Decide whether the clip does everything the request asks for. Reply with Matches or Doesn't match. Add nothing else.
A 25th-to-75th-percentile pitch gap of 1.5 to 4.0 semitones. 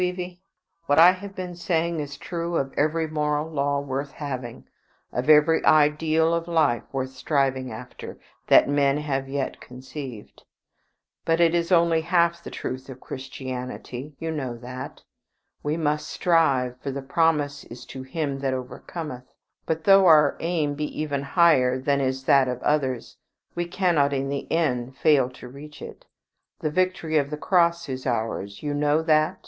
Matches